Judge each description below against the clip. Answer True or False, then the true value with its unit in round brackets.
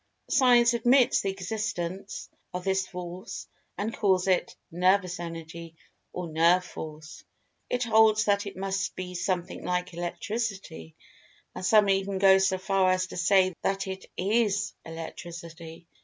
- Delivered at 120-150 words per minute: True (140 wpm)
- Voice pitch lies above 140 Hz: True (190 Hz)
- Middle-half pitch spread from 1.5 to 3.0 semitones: True (2.4 semitones)